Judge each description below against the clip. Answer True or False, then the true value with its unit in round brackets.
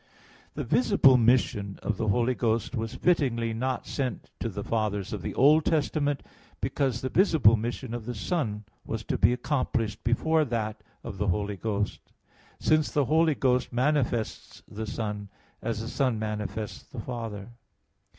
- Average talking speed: True (160 wpm)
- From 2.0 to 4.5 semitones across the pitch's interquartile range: True (3.8 semitones)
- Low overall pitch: True (115 Hz)